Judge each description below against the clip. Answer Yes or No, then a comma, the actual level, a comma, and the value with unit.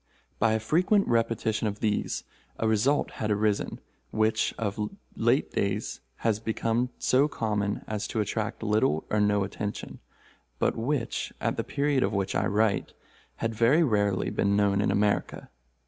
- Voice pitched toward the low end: Yes, low, 110 Hz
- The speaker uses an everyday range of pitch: No, narrow, 1.9 semitones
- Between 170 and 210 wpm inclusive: No, average, 155 wpm